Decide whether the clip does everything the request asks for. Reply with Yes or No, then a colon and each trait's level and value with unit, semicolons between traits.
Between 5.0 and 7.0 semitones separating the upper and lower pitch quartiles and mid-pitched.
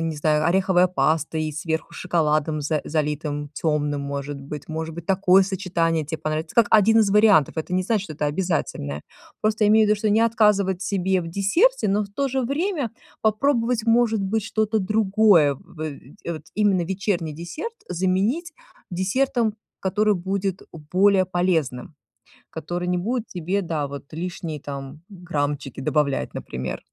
Yes: average, 5.3 semitones; medium, 180 Hz